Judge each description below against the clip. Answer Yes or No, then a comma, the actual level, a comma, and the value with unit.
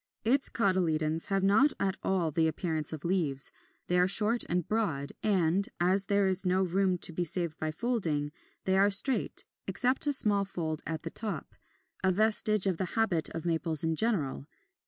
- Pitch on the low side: No, medium, 185 Hz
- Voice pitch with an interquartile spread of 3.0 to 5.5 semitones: Yes, average, 3.9 semitones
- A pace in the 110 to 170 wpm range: No, average, 180 wpm